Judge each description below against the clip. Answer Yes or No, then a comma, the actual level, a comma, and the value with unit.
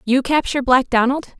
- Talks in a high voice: Yes, very high, 260 Hz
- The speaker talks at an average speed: Yes, average, 175 wpm